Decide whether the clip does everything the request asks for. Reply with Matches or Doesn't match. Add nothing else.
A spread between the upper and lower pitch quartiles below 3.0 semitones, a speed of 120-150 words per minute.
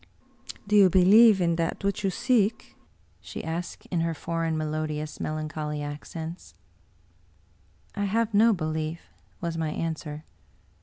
Doesn't match